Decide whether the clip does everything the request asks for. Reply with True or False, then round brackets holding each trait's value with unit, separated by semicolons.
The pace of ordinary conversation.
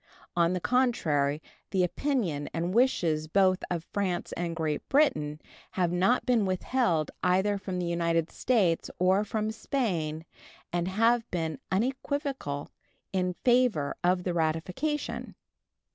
False (130 wpm)